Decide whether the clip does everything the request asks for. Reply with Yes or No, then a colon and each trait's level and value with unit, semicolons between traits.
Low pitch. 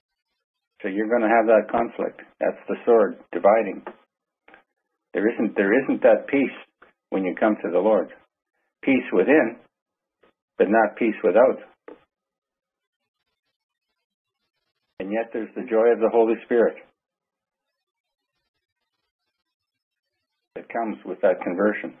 Yes: low, 115 Hz